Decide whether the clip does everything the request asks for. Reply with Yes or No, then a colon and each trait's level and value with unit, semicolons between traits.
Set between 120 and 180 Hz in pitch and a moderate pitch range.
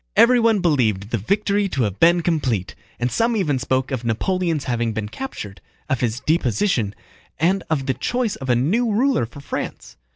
No: medium, 140 Hz; wide, 8.9 semitones